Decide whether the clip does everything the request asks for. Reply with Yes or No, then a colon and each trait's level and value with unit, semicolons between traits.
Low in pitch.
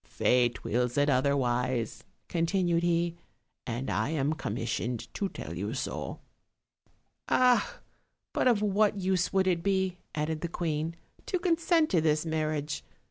No: medium, 160 Hz